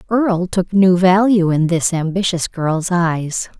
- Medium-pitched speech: Yes, medium, 180 Hz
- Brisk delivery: No, average, 150 wpm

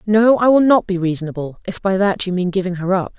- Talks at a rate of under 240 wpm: No, fast, 265 wpm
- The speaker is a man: No, female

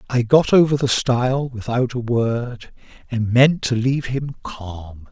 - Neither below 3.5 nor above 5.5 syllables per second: Yes, 4.2 syllables/s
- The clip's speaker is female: No, male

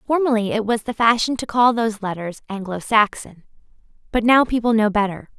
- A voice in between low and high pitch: No, high, 220 Hz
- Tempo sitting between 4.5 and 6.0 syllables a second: Yes, 5.6 syllables/s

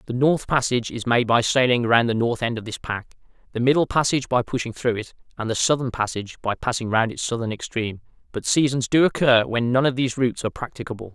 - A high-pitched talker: No, low, 120 Hz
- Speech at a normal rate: No, fast, 225 wpm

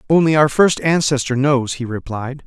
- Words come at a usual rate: Yes, average, 170 wpm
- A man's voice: Yes, male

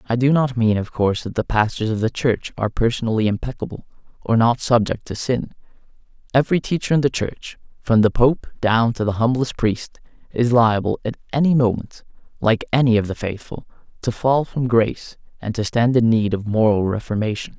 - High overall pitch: No, low, 115 Hz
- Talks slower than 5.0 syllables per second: No, 5.5 syllables/s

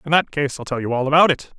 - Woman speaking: No, male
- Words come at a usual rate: No, fast, 340 wpm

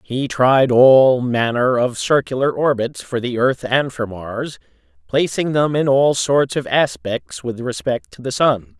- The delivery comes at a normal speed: Yes, average, 170 wpm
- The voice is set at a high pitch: No, low, 125 Hz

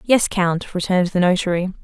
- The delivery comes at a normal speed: Yes, average, 165 wpm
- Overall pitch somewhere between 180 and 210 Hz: Yes, medium, 185 Hz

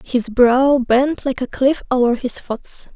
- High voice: Yes, very high, 255 Hz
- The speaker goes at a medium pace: Yes, average, 185 wpm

